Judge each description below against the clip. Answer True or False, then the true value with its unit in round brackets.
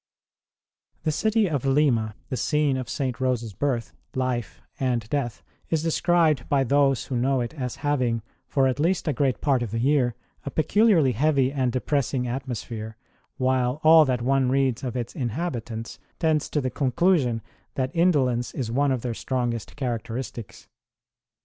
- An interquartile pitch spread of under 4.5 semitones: True (3.3 semitones)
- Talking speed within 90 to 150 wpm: False (160 wpm)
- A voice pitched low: True (130 Hz)